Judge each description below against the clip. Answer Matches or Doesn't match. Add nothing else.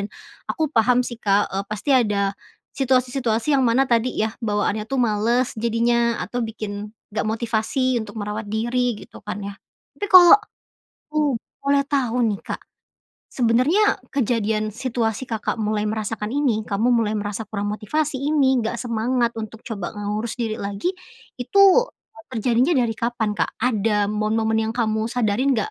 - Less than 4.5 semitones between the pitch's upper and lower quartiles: Matches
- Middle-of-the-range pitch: Doesn't match